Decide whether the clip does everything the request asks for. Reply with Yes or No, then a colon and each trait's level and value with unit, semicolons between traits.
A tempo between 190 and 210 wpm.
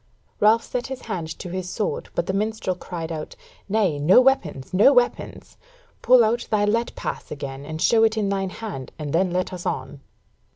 Yes: average, 195 wpm